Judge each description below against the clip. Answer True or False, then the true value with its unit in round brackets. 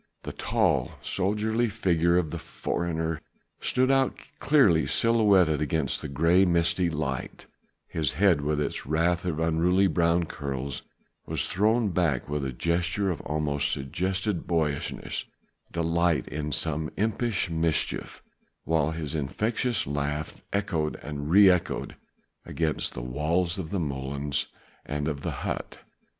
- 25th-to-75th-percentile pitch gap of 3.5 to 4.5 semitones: True (3.8 semitones)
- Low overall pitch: True (80 Hz)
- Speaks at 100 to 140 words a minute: True (135 wpm)